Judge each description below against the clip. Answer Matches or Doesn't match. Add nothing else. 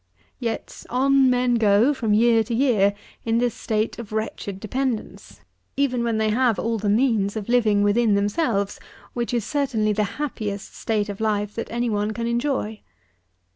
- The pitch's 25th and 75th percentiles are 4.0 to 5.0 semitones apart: Doesn't match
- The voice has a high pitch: Matches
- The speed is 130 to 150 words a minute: Doesn't match